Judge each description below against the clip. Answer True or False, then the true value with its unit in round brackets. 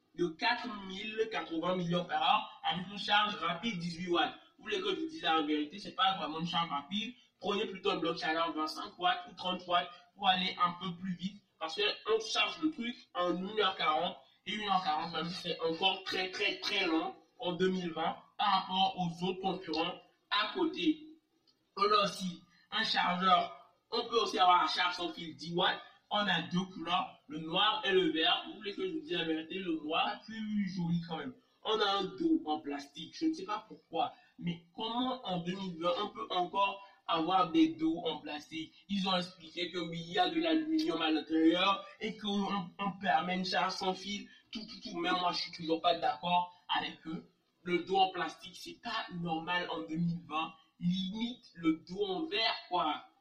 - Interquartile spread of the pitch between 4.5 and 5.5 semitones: True (4.9 semitones)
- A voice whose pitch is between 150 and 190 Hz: True (185 Hz)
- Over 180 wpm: True (195 wpm)